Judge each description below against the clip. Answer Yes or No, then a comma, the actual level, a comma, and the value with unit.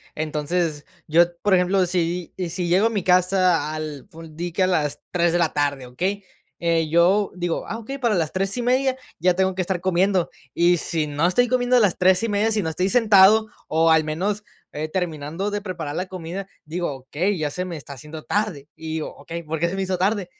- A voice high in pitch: No, medium, 175 Hz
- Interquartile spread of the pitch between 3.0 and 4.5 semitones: Yes, average, 3.4 semitones